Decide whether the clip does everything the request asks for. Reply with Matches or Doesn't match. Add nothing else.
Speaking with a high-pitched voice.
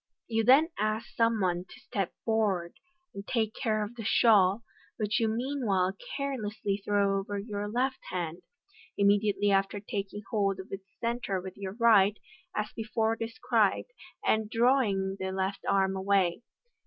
Matches